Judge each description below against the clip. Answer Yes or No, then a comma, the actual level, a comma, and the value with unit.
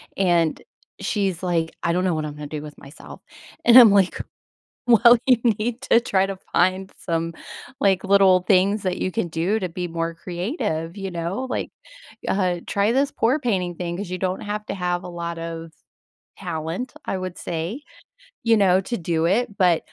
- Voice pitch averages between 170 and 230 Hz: Yes, medium, 185 Hz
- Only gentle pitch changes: No, average, 3.3 semitones